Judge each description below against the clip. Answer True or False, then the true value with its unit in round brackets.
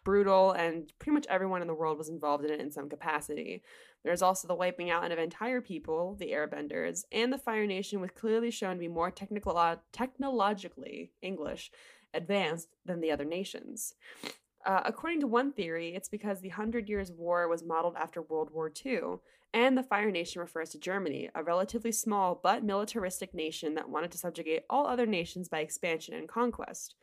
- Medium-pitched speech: True (180 Hz)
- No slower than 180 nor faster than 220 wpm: True (190 wpm)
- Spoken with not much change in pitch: False (4.4 semitones)